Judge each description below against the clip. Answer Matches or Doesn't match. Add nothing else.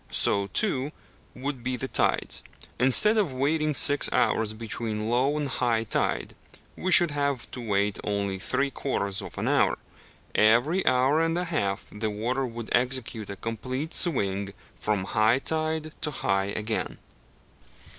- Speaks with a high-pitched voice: Doesn't match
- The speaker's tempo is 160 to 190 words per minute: Doesn't match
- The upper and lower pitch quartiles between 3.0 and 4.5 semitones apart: Doesn't match